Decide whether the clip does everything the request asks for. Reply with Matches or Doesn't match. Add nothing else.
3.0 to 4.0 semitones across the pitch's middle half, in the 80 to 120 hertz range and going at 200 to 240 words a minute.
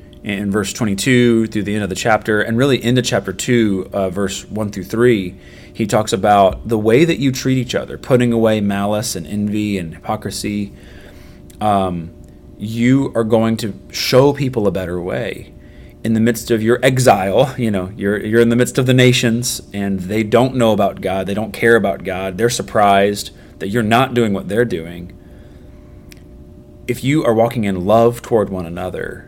Doesn't match